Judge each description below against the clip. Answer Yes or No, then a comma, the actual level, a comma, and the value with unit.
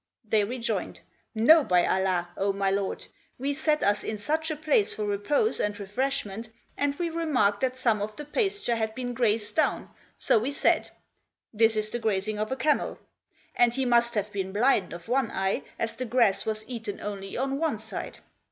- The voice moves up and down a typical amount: Yes, average, 4.6 semitones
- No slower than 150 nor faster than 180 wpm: No, average, 195 wpm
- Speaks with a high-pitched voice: Yes, high, 225 Hz